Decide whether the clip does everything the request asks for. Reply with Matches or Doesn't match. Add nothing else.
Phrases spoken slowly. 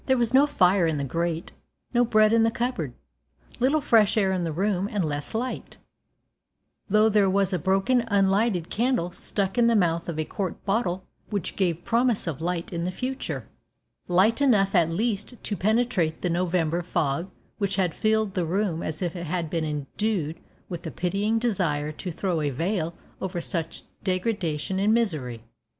Doesn't match